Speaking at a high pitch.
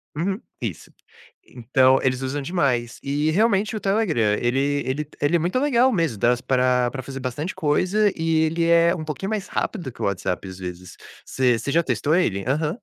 No: medium, 145 Hz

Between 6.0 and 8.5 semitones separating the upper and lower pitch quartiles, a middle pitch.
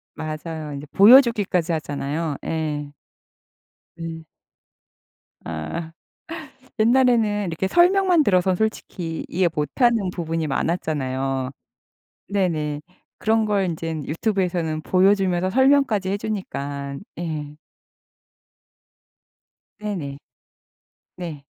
No: average, 5.3 semitones; medium, 170 Hz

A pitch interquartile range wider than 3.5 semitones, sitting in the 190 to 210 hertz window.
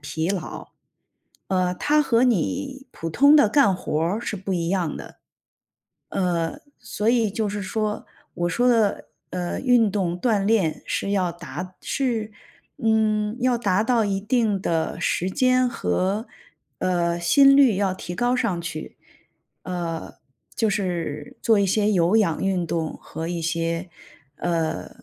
Yes: average, 4.7 semitones; high, 195 Hz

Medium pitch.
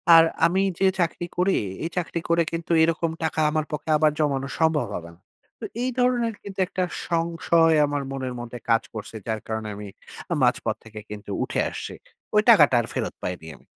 Yes: medium, 160 Hz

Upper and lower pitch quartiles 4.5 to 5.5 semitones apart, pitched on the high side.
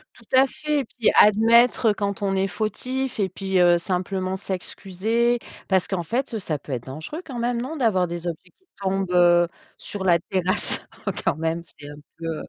Yes: average, 5.0 semitones; high, 195 Hz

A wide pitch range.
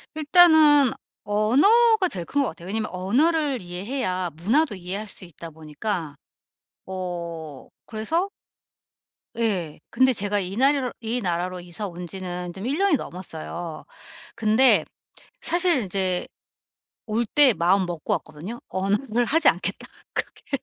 Yes: wide, 7.0 semitones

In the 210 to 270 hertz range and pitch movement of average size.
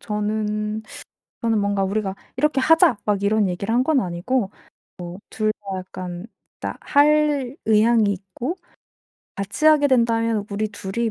Yes: high, 215 Hz; average, 3.5 semitones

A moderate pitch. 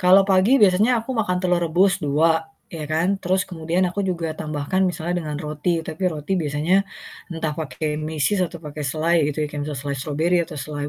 Yes: medium, 165 Hz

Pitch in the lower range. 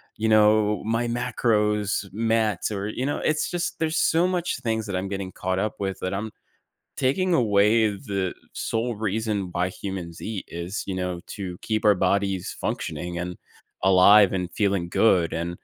Yes: low, 105 Hz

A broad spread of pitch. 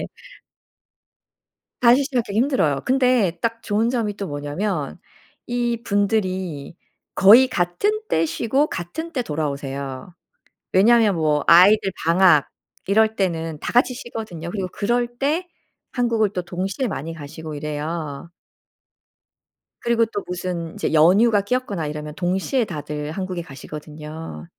Yes: wide, 6.6 semitones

